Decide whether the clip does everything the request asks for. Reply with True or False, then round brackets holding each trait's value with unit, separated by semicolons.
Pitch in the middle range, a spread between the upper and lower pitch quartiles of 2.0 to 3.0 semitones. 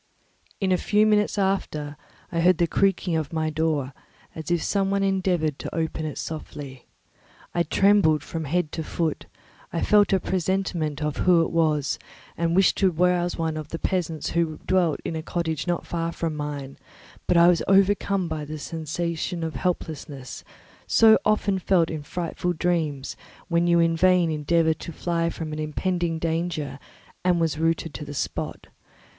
True (165 Hz; 2.5 semitones)